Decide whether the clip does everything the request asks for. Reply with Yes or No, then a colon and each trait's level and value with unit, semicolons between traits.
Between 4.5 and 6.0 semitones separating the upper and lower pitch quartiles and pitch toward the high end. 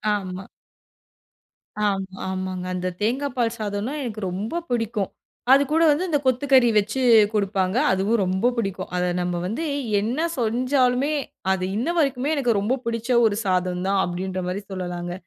Yes: average, 5.1 semitones; high, 215 Hz